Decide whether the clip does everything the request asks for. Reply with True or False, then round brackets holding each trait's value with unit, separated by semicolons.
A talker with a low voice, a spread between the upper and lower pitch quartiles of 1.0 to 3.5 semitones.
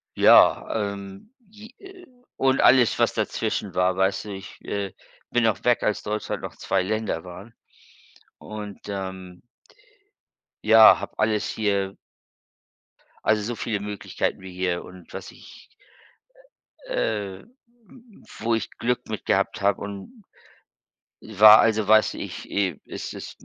True (105 Hz; 2.6 semitones)